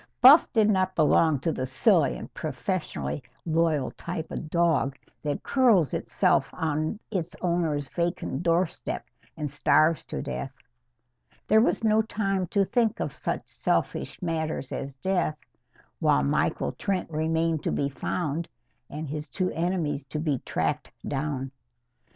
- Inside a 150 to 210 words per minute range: No, average, 140 wpm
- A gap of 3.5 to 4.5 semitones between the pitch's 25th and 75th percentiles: Yes, average, 3.9 semitones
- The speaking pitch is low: No, medium, 160 Hz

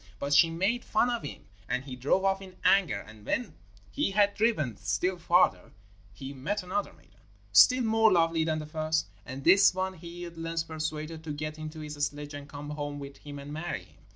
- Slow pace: No, fast, 205 wpm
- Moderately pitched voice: Yes, medium, 155 Hz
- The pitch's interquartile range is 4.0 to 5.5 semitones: Yes, average, 4.4 semitones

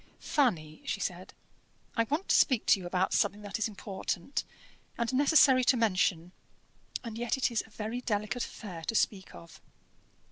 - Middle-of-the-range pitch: No, high, 220 Hz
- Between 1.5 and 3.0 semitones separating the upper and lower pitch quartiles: No, average, 4.5 semitones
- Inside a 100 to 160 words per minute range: No, average, 170 wpm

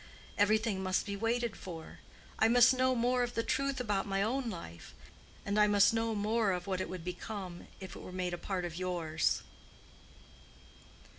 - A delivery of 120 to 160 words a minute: No, average, 180 wpm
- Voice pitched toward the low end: No, high, 205 Hz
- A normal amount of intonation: Yes, average, 3.9 semitones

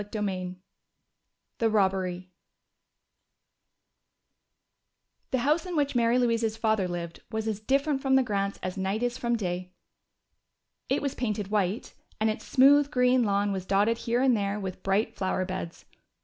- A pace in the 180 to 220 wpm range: No, average, 150 wpm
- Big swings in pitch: No, average, 4.3 semitones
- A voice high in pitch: Yes, high, 215 Hz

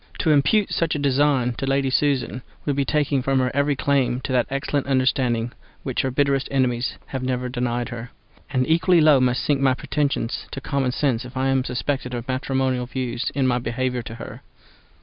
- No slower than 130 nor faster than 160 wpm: No, average, 195 wpm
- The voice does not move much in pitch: Yes, narrow, 2.0 semitones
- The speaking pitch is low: Yes, low, 130 Hz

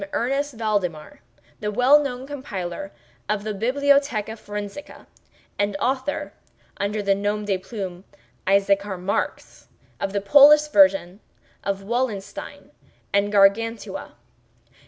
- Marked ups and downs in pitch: No, average, 4.7 semitones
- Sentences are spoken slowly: Yes, slow, 115 wpm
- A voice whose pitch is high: Yes, high, 210 Hz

